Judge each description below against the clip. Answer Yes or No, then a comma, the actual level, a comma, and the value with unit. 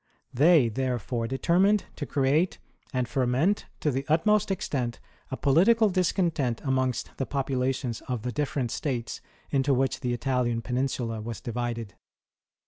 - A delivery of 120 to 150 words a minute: Yes, slow, 135 wpm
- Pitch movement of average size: Yes, average, 3.7 semitones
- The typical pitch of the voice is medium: No, low, 130 Hz